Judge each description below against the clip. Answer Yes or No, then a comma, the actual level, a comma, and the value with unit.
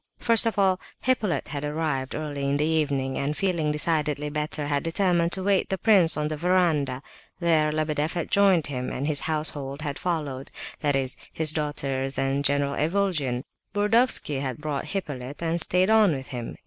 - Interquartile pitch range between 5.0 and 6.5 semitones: No, average, 3.7 semitones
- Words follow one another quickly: No, average, 175 wpm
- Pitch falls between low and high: Yes, medium, 150 Hz